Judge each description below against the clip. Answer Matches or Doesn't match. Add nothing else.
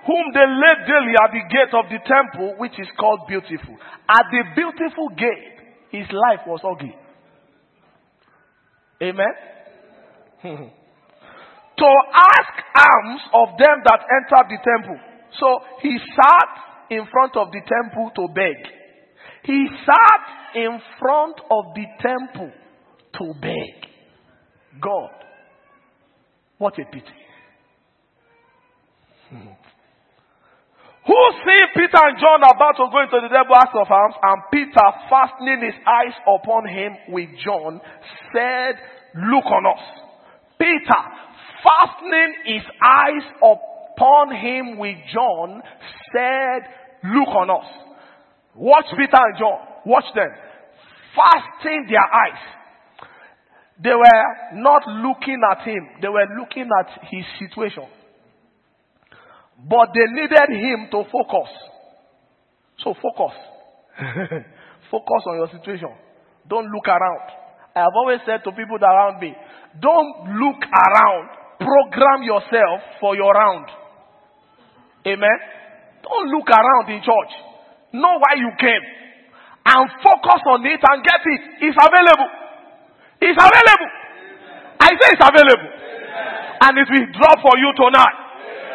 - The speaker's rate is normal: Doesn't match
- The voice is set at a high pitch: Matches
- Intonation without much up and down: Doesn't match